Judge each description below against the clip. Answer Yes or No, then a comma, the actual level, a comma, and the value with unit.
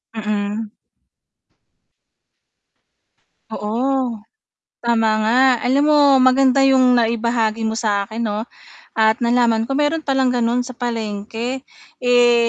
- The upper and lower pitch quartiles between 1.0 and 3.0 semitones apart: Yes, narrow, 2.5 semitones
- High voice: Yes, high, 235 Hz